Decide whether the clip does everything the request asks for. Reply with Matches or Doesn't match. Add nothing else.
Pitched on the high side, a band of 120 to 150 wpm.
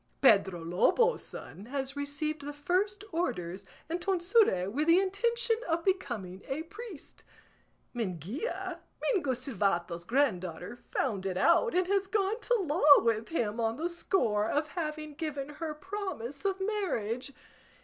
Matches